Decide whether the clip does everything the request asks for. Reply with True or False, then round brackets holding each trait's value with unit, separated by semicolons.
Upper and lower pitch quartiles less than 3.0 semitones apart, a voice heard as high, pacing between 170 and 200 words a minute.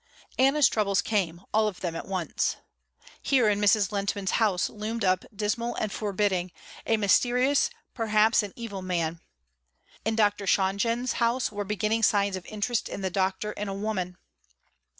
False (2.6 semitones; 205 Hz; 155 wpm)